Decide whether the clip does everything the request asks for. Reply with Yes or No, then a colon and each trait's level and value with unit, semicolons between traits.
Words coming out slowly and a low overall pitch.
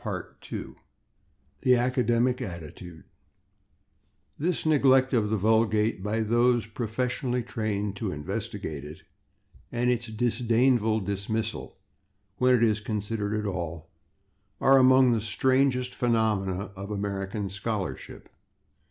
Yes: slow, 110 wpm; low, 110 Hz